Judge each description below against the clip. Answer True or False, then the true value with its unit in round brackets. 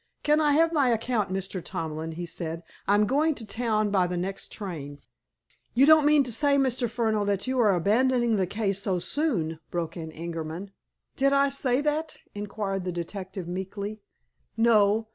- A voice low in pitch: False (205 Hz)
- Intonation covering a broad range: True (6.1 semitones)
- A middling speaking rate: True (175 wpm)